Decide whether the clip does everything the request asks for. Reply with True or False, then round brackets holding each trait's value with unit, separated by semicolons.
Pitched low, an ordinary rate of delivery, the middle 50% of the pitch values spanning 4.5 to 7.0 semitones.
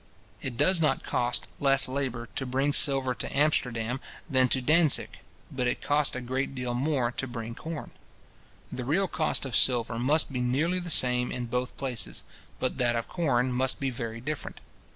False (130 Hz; 180 wpm; 2.8 semitones)